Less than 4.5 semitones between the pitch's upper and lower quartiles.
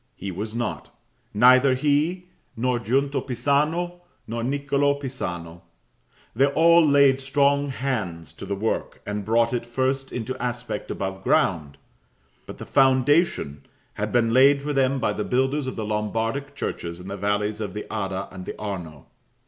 No: average, 5.1 semitones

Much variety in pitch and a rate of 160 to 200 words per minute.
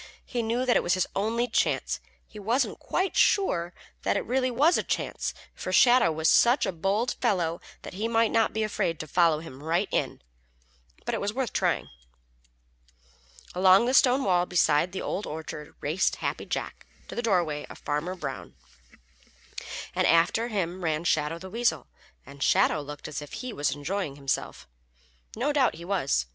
Yes: wide, 6.4 semitones; average, 180 wpm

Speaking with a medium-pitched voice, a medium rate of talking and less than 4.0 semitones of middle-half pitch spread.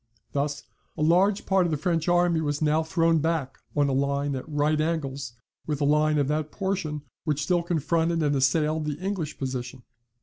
Yes: medium, 155 Hz; average, 190 wpm; average, 2.7 semitones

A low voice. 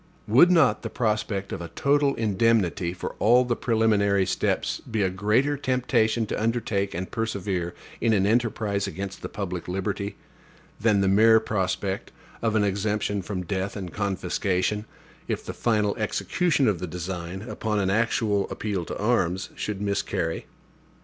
Yes: low, 105 Hz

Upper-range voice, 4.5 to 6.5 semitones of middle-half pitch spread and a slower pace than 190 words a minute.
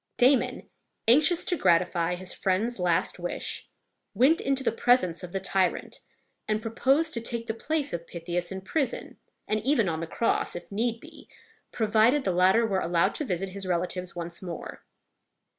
Yes: high, 200 Hz; wide, 5.4 semitones; average, 170 wpm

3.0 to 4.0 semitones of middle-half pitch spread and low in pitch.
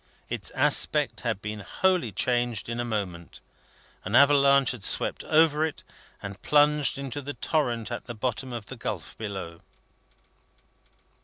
No: average, 5.3 semitones; low, 120 Hz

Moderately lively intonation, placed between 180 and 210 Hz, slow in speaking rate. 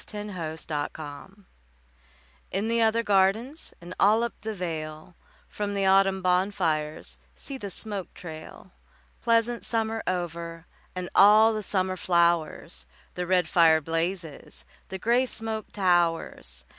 Yes: average, 4.5 semitones; medium, 185 Hz; slow, 130 wpm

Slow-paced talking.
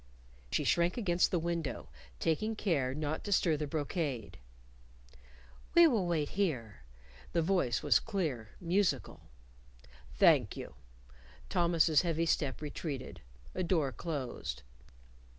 Yes: slow, 115 wpm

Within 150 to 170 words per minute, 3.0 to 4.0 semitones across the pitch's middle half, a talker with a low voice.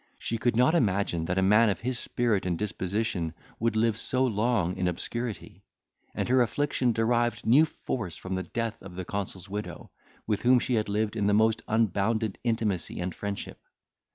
No: average, 180 wpm; average, 3.5 semitones; low, 110 Hz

